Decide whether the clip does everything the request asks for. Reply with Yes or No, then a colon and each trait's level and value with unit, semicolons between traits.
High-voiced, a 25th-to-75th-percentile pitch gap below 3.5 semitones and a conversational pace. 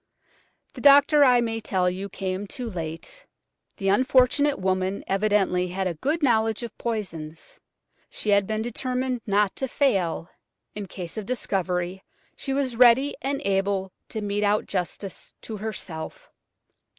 No: high, 210 Hz; average, 4.8 semitones; average, 145 wpm